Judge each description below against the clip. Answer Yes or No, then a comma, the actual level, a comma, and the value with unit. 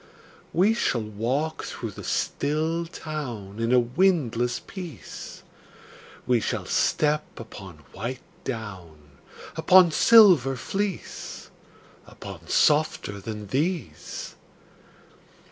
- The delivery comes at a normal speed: No, slow, 95 wpm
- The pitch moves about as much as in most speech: No, wide, 6.9 semitones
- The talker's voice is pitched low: Yes, low, 130 Hz